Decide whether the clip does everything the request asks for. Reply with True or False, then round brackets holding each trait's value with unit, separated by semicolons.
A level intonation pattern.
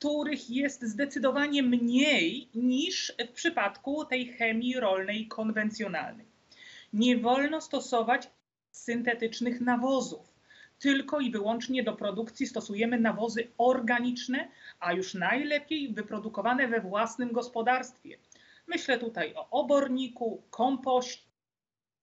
False (3.1 semitones)